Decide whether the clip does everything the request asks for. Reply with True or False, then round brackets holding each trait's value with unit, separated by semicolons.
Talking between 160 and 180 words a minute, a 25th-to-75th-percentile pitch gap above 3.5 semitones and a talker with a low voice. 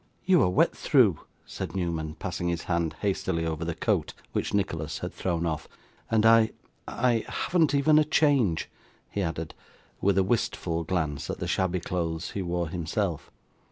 True (165 wpm; 4.5 semitones; 90 Hz)